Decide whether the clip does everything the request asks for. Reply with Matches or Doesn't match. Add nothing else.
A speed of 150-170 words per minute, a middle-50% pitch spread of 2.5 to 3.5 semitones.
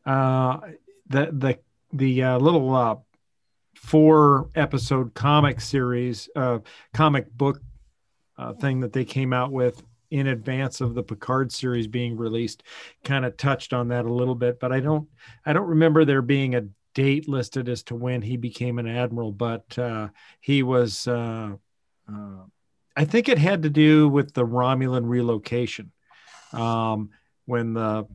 Matches